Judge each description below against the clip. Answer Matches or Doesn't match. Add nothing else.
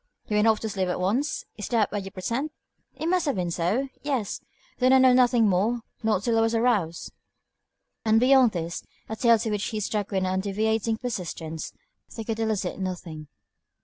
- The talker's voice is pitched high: Matches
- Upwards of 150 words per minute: Matches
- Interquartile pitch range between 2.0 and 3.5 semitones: Doesn't match